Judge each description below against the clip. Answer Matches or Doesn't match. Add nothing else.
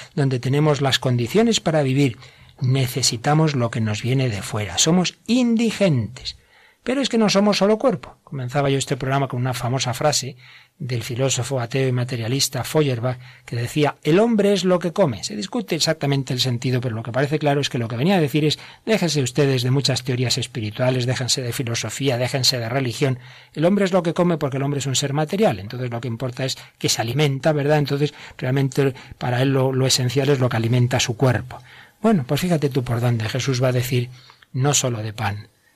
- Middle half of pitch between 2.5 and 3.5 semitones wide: Matches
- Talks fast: Matches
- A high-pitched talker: Doesn't match